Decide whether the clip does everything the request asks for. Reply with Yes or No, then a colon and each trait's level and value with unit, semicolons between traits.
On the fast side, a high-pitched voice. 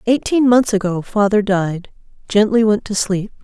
No: average, 140 wpm; high, 210 Hz